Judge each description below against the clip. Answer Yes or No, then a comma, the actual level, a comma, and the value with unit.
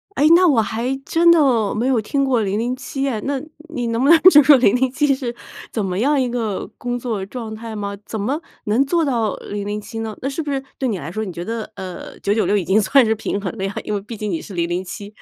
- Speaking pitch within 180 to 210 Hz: No, high, 230 Hz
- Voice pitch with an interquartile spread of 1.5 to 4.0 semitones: No, average, 4.6 semitones